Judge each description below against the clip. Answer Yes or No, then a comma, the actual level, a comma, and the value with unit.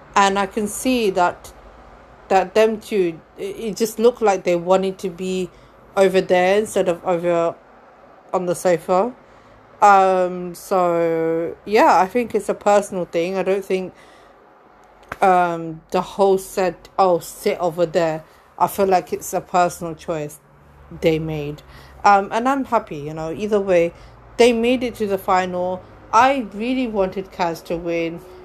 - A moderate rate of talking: Yes, average, 155 wpm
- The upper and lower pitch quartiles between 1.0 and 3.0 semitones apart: Yes, average, 2.7 semitones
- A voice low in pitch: No, medium, 185 Hz